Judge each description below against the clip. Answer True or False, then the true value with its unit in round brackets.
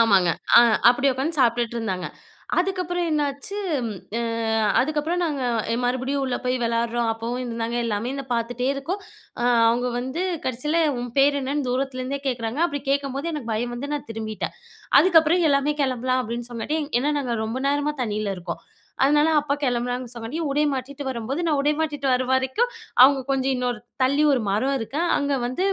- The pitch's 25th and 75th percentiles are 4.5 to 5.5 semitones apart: False (3.5 semitones)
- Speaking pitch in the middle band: False (260 Hz)